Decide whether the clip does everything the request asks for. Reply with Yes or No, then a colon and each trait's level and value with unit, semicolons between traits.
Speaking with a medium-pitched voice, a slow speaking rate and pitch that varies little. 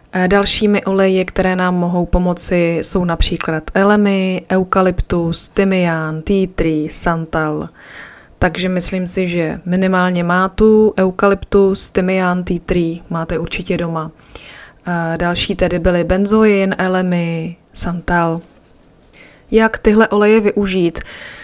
Yes: medium, 180 Hz; slow, 105 wpm; narrow, 2.2 semitones